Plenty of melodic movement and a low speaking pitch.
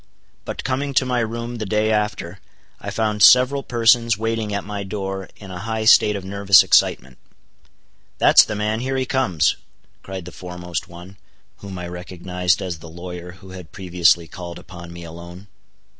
No: average, 3.8 semitones; very low, 95 Hz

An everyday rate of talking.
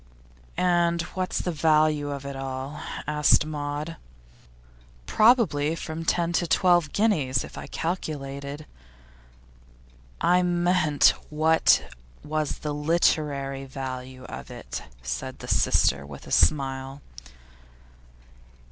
No: slow, 105 wpm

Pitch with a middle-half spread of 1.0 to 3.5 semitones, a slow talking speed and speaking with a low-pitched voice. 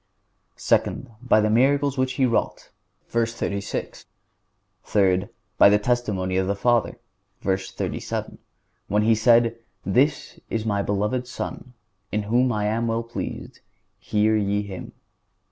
Yes: average, 3.1 semitones; slow, 130 wpm; low, 110 Hz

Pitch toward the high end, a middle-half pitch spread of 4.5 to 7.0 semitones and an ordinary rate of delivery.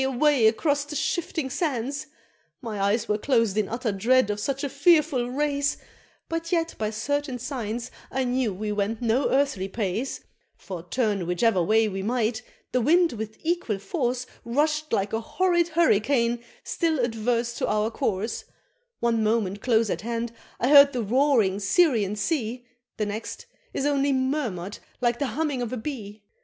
Yes: high, 240 Hz; average, 4.8 semitones; average, 165 wpm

